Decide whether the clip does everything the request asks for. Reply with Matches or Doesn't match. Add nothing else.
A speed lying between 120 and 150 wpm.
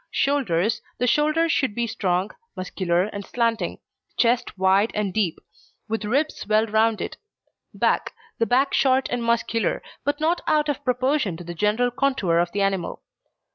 Doesn't match